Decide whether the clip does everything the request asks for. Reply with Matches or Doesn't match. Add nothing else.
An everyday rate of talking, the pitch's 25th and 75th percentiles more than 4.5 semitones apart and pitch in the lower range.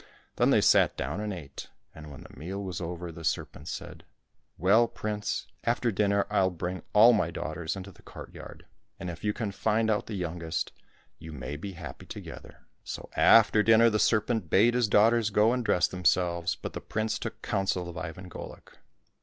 Doesn't match